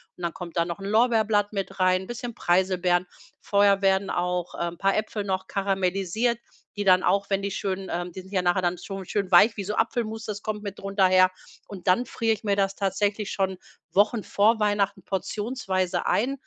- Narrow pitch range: Yes, narrow, 2.1 semitones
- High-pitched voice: Yes, high, 195 Hz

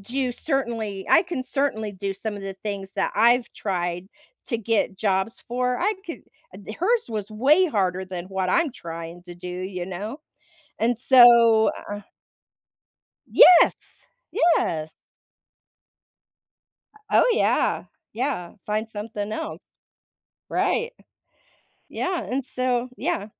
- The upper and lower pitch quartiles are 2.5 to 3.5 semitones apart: No, average, 4.8 semitones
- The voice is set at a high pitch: Yes, high, 220 Hz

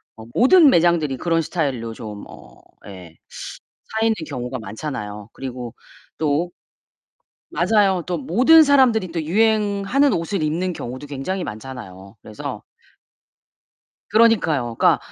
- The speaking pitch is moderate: Yes, medium, 160 Hz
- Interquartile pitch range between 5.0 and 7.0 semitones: No, wide, 8.7 semitones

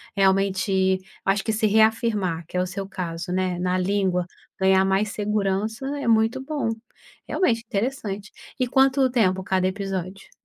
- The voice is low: No, high, 195 Hz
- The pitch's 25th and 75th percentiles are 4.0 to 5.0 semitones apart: No, average, 2.8 semitones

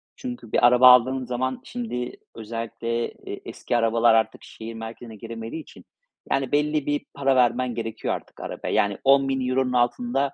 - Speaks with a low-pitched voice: Yes, low, 125 Hz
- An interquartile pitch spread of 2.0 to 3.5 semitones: Yes, average, 2.7 semitones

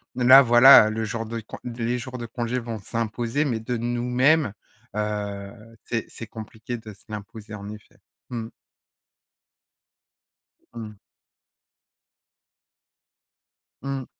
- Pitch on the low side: Yes, low, 115 Hz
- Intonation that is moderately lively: No, narrow, 2.2 semitones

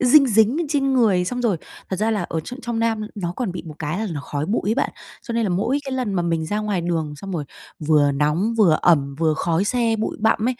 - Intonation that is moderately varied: No, wide, 6.0 semitones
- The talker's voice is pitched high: Yes, high, 200 Hz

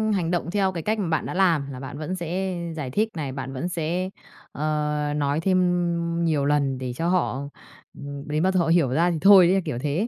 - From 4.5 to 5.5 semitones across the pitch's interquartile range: No, average, 3.9 semitones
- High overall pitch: No, medium, 165 Hz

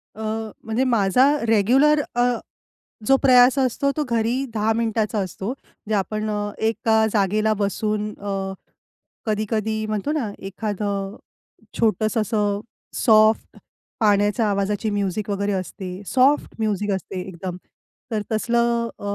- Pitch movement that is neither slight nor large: No, narrow, 2.2 semitones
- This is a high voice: Yes, high, 215 Hz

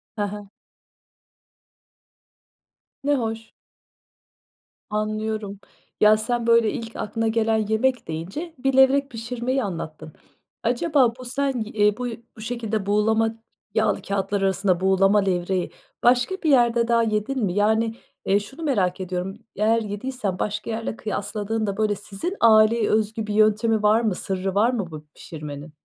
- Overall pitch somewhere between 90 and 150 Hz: No, high, 215 Hz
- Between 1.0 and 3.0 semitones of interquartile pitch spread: Yes, average, 2.7 semitones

